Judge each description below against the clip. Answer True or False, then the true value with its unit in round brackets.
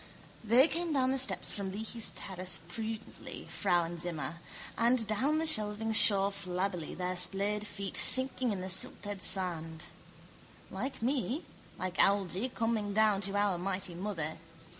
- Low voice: False (200 Hz)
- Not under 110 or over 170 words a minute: True (140 wpm)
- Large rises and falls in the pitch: False (3.8 semitones)